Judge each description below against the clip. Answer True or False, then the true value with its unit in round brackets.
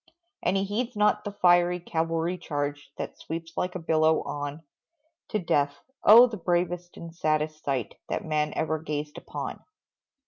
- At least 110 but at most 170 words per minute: True (160 wpm)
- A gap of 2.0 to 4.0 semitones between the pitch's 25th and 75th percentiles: True (2.8 semitones)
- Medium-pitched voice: True (165 Hz)